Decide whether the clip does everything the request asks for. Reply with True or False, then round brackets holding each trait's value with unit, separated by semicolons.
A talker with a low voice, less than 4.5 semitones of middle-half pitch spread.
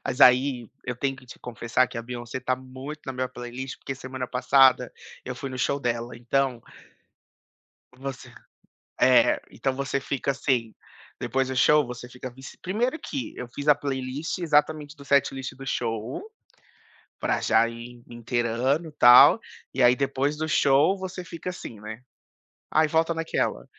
True (130 Hz; 2.6 semitones)